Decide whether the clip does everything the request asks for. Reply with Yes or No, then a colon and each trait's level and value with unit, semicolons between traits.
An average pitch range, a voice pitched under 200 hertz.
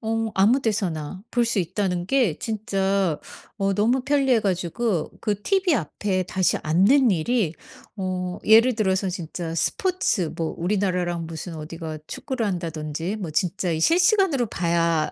Yes: average, 4.9 semitones; high, 190 Hz